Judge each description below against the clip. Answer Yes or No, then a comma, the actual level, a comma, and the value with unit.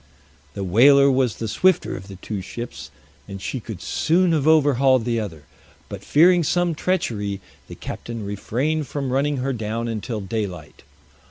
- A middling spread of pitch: No, wide, 5.7 semitones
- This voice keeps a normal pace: Yes, average, 160 wpm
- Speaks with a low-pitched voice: Yes, low, 120 Hz